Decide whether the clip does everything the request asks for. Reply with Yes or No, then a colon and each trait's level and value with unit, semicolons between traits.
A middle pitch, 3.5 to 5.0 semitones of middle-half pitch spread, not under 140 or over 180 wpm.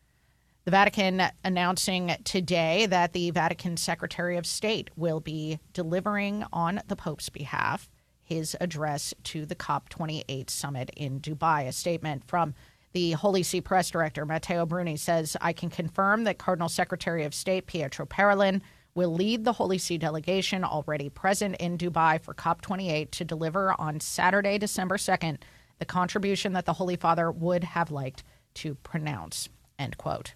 No: medium, 175 Hz; average, 2.9 semitones; average, 150 wpm